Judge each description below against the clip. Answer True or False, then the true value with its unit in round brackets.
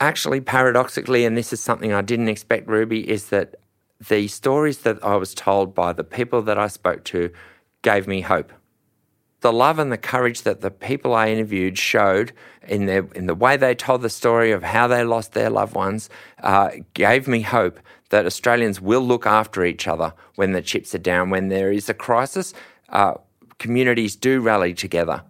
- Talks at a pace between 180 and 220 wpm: True (190 wpm)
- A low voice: True (110 Hz)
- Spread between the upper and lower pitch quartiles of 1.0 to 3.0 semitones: False (3.7 semitones)